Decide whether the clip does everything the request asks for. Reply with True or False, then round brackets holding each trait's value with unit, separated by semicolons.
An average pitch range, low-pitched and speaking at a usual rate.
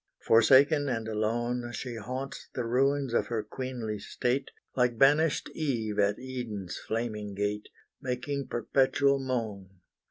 False (3.4 semitones; 120 Hz; 125 wpm)